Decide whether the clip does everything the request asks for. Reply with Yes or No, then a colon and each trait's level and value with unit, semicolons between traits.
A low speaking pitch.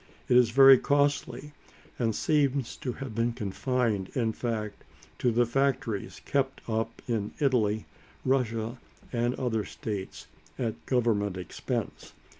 Yes: low, 120 Hz